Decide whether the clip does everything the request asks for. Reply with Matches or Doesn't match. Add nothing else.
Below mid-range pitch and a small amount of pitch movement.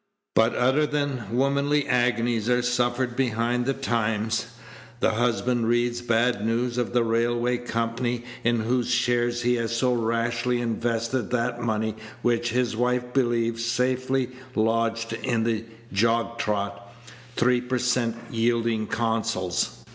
Matches